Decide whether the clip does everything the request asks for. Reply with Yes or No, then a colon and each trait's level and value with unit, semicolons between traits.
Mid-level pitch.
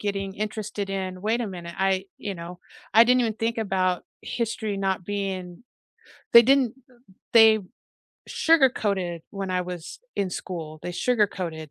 No: high, 195 Hz